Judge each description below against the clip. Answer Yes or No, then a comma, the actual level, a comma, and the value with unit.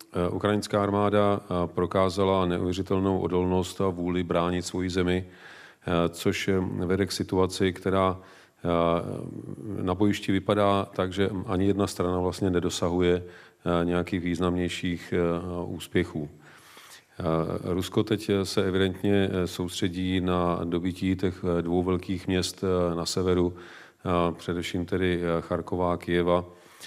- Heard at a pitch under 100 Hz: Yes, very low, 90 Hz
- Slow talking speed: Yes, slow, 105 wpm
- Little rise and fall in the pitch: Yes, narrow, 1.5 semitones